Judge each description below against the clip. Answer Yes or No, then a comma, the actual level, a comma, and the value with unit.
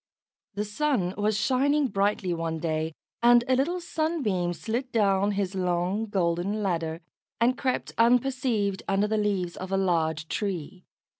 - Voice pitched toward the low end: No, high, 200 Hz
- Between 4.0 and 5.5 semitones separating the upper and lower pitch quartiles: Yes, average, 5.1 semitones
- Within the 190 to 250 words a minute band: No, average, 145 wpm